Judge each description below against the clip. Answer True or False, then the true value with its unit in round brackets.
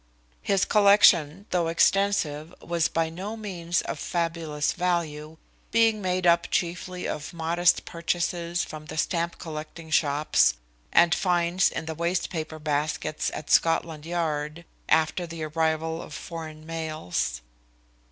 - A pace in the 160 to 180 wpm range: False (135 wpm)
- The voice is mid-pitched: True (165 Hz)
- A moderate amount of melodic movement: False (2.0 semitones)